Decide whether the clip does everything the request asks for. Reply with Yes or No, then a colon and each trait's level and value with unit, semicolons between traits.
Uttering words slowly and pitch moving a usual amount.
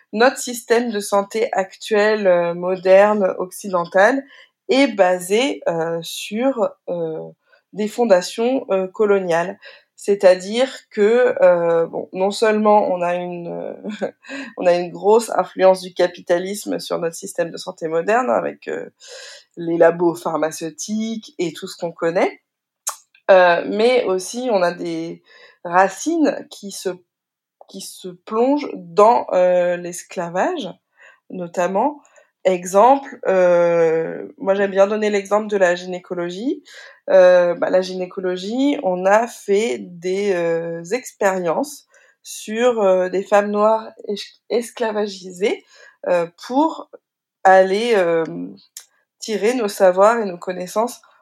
Yes: slow, 120 wpm; average, 4.4 semitones